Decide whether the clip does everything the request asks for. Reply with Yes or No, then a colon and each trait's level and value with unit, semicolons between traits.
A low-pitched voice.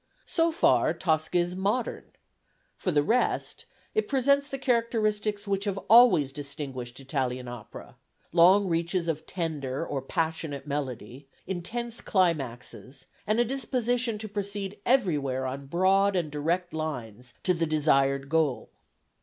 No: medium, 170 Hz